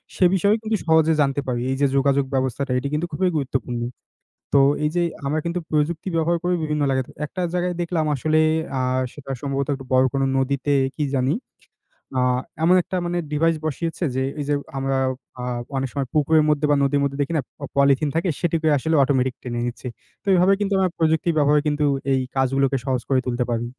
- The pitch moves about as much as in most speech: Yes, average, 3.5 semitones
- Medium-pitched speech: Yes, medium, 145 Hz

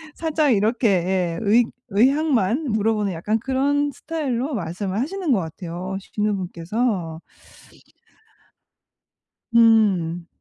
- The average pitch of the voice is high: Yes, high, 215 Hz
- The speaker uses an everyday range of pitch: No, wide, 6.0 semitones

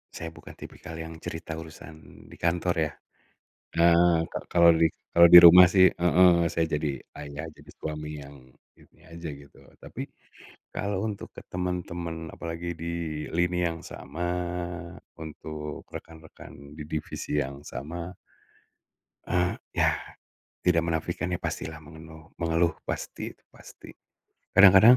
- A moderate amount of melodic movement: No, narrow, 1.8 semitones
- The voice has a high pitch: No, very low, 85 Hz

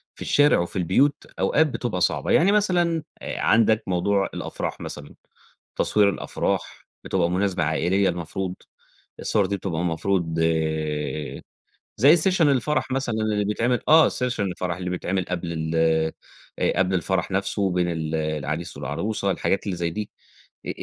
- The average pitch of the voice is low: Yes, very low, 95 Hz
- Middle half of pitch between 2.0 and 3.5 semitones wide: No, average, 5.1 semitones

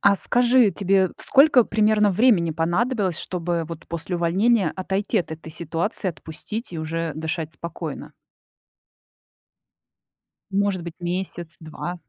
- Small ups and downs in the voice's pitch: No, average, 3.8 semitones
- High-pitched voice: No, medium, 180 Hz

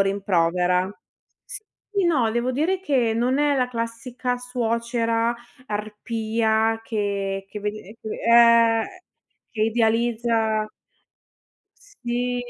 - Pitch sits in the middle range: No, high, 230 Hz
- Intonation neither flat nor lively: No, narrow, 2.3 semitones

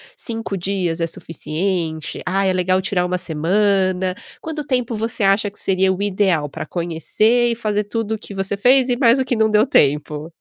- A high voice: Yes, high, 195 Hz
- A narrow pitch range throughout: No, average, 3.8 semitones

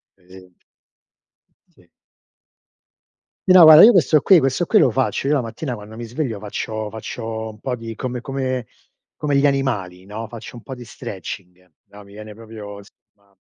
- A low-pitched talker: Yes, low, 115 Hz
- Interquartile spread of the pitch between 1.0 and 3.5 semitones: No, average, 4.3 semitones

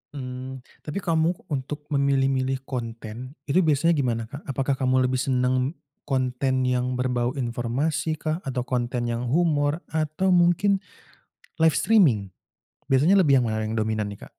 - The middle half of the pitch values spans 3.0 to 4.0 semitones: Yes, average, 3.7 semitones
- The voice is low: Yes, low, 130 Hz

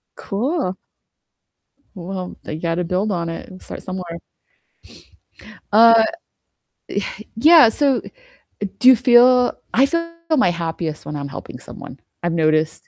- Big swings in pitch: Yes, wide, 6.7 semitones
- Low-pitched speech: No, high, 190 Hz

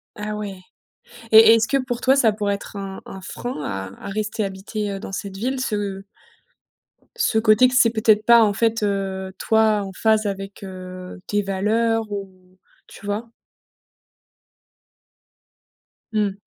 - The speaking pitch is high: Yes, high, 210 Hz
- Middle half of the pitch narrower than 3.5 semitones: Yes, narrow, 2.4 semitones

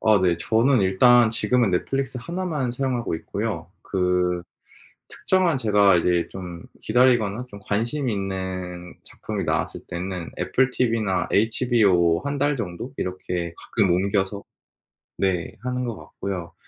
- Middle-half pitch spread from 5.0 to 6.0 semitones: Yes, wide, 5.5 semitones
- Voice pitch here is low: Yes, low, 100 Hz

